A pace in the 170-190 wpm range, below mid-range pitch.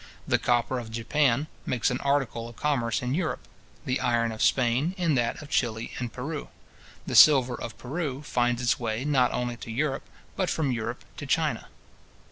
Yes: average, 180 wpm; low, 125 Hz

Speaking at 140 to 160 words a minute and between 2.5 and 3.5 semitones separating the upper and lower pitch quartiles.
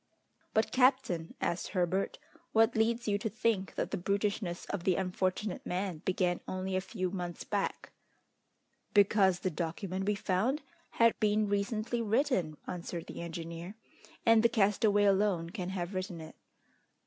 Yes: average, 150 wpm; average, 3.2 semitones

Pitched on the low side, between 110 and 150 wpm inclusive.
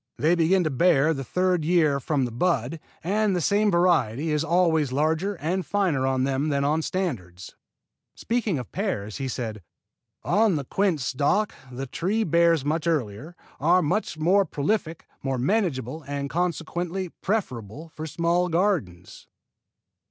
No: medium, 160 Hz; average, 145 wpm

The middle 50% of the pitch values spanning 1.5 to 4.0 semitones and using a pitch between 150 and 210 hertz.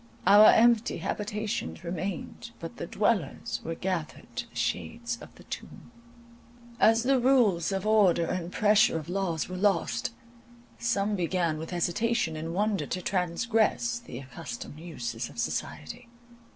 No: average, 4.8 semitones; medium, 185 Hz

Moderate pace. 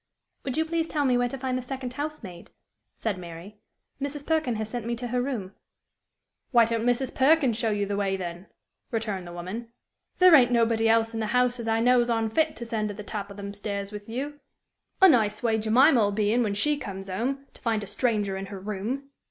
No: fast, 230 wpm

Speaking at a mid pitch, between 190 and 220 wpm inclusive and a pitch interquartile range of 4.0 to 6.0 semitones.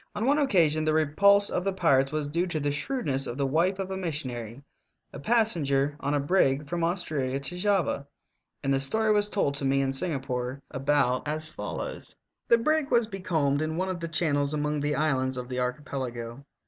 Yes: medium, 150 Hz; average, 200 wpm; average, 5.1 semitones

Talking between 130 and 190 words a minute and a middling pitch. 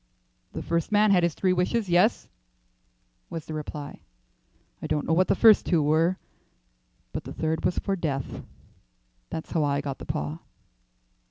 Yes: average, 165 wpm; medium, 165 Hz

